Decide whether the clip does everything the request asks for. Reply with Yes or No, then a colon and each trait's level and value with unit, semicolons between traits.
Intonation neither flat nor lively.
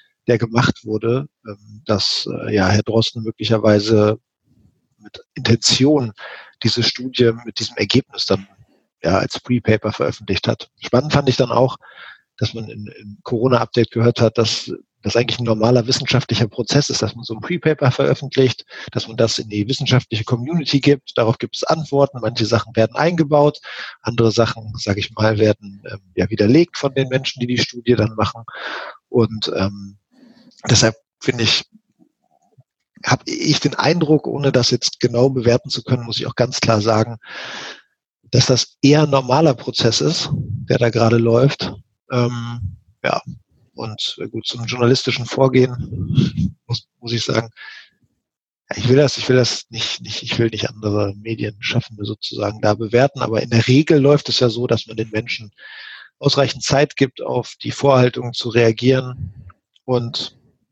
Yes: average, 3.0 semitones